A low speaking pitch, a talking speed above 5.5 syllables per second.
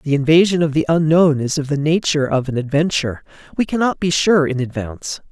No: medium, 150 Hz; 6.0 syllables/s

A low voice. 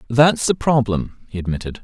Yes: low, 120 Hz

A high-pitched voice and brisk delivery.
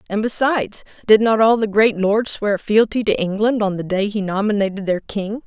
Yes: high, 210 Hz; fast, 210 wpm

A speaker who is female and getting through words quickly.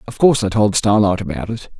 No: male; fast, 235 wpm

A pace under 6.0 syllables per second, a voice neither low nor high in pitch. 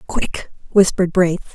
Yes: 4.9 syllables/s; medium, 180 Hz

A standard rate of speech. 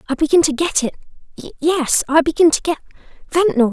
No: slow, 130 wpm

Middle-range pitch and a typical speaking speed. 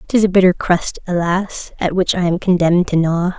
No: medium, 180 Hz; fast, 215 wpm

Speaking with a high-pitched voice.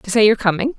Yes: high, 215 Hz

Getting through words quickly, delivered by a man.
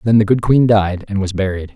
Yes: fast, 275 wpm; male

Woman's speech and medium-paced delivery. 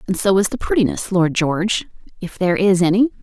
Yes: female; average, 185 wpm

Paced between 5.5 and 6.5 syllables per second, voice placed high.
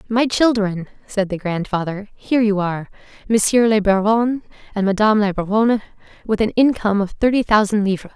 Yes: 5.8 syllables/s; high, 210 Hz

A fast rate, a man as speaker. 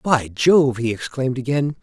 No: average, 165 wpm; male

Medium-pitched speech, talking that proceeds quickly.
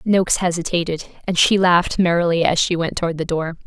No: medium, 175 Hz; average, 195 wpm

